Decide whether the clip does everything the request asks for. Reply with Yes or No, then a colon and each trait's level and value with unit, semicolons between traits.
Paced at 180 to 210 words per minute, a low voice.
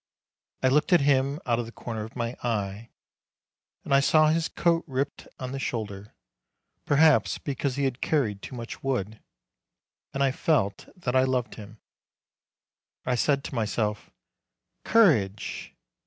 No: average, 150 wpm; low, 130 Hz